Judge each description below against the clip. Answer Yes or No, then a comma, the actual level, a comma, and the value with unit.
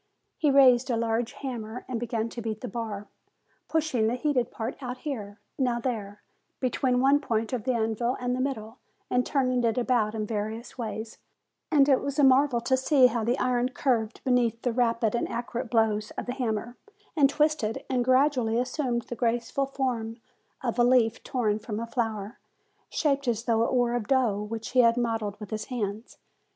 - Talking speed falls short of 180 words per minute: No, average, 190 wpm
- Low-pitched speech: No, high, 240 Hz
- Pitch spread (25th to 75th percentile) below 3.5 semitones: Yes, narrow, 2.4 semitones